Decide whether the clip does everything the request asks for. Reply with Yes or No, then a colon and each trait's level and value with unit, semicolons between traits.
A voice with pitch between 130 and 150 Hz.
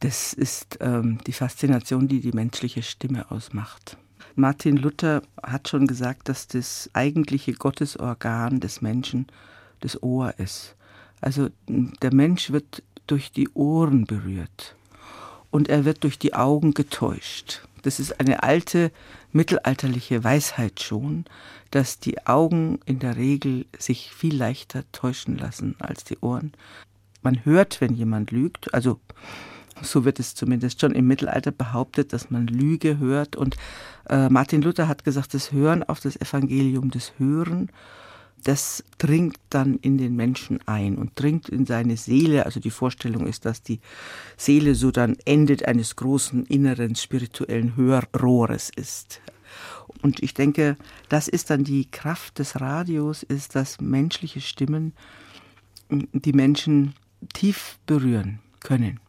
Yes: low, 135 Hz